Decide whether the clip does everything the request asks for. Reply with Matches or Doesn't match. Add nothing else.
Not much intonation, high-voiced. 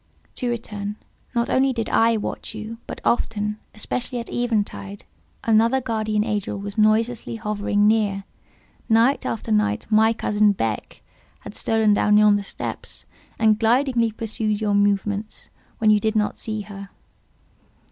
Matches